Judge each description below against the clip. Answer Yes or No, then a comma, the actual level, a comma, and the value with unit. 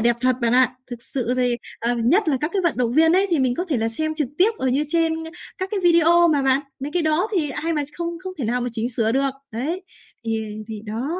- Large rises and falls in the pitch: Yes, wide, 5.7 semitones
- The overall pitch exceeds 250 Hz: Yes, very high, 275 Hz